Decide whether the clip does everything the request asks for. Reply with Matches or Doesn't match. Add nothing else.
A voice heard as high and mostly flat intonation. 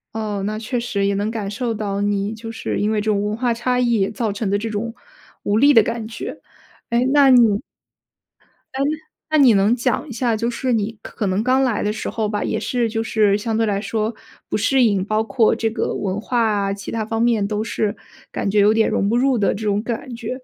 Matches